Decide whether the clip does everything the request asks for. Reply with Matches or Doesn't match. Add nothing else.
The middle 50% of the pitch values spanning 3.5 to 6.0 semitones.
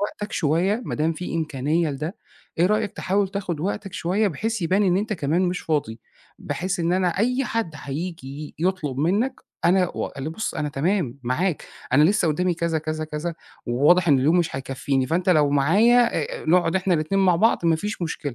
Matches